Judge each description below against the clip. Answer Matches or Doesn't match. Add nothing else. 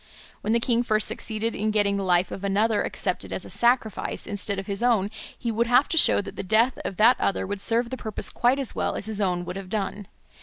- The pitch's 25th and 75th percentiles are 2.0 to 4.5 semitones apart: Matches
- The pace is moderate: Doesn't match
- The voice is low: Doesn't match